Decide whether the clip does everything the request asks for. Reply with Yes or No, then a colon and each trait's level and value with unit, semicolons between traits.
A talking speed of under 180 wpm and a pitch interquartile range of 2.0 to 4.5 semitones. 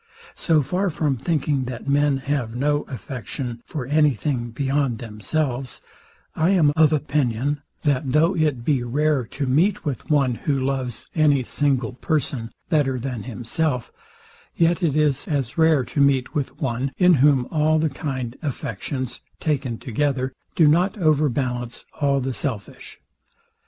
Yes: average, 145 wpm; average, 3.3 semitones